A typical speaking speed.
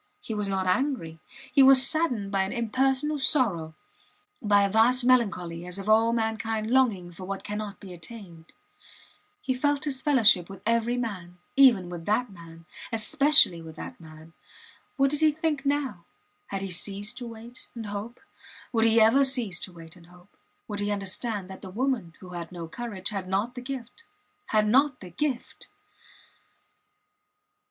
Yes: average, 170 wpm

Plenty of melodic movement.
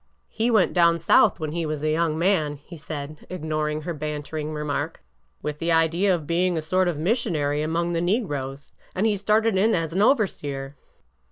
No: average, 3.4 semitones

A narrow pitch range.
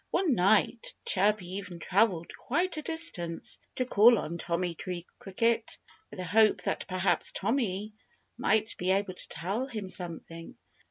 No: average, 4.2 semitones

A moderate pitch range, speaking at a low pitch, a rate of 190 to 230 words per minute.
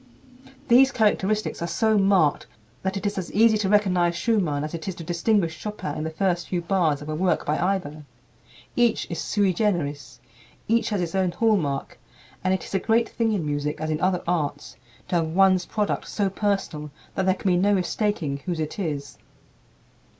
No: average, 4.4 semitones; medium, 185 Hz; average, 195 wpm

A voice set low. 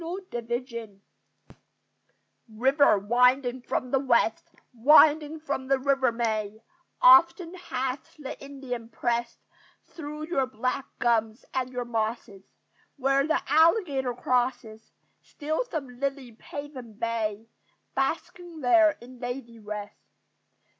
No: very high, 255 Hz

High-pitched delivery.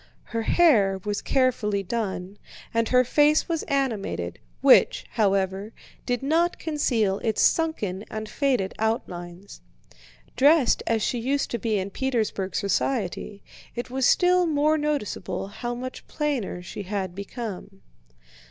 Yes: high, 230 Hz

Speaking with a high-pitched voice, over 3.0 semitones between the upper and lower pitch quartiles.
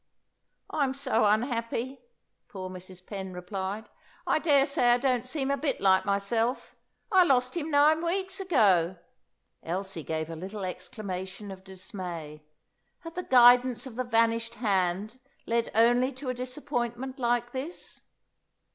Yes: high, 235 Hz; wide, 5.5 semitones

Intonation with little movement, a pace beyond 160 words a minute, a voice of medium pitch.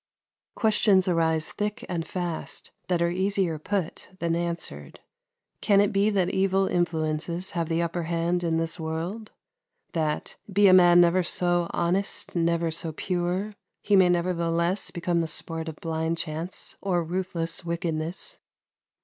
No: narrow, 2.2 semitones; average, 145 wpm; medium, 175 Hz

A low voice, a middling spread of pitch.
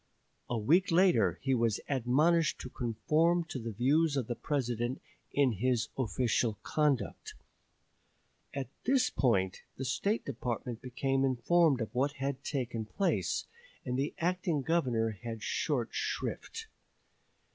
Yes: low, 130 Hz; average, 4.5 semitones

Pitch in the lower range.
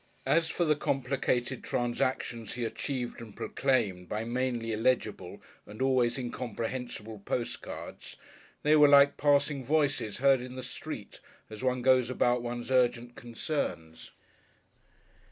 Yes: low, 125 Hz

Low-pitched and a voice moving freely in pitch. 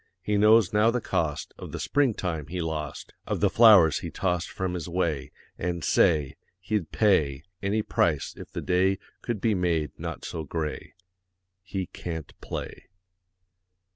No: very low, 90 Hz; average, 4.4 semitones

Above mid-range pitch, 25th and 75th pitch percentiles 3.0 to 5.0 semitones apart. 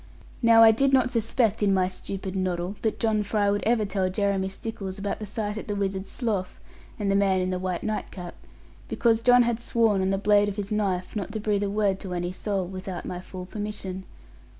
No: high, 200 Hz; narrow, 2.4 semitones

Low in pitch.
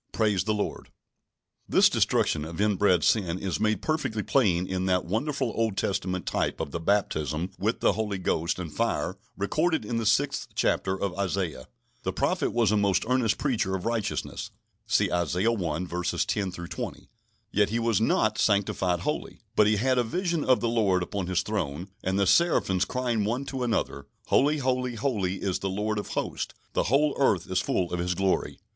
Yes: low, 100 Hz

